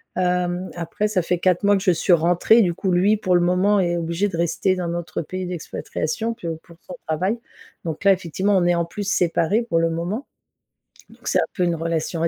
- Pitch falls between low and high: Yes, medium, 180 Hz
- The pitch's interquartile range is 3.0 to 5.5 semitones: No, narrow, 2.5 semitones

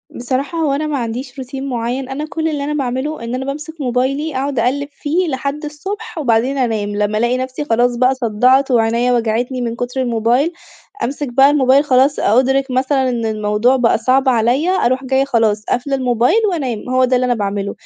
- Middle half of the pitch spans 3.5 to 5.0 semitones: No, average, 2.8 semitones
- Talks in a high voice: Yes, very high, 260 Hz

